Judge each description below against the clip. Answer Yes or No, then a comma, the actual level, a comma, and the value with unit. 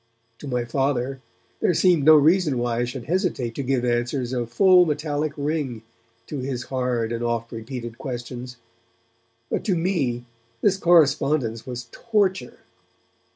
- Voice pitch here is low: Yes, low, 130 Hz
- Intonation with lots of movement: No, average, 4.4 semitones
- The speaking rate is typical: Yes, average, 145 wpm